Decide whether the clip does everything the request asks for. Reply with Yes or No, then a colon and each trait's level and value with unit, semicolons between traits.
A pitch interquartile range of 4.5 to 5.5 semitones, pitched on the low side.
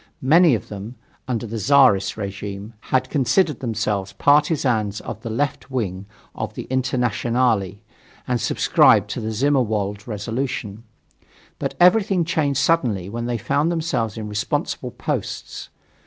Yes: average, 5.0 semitones; low, 120 Hz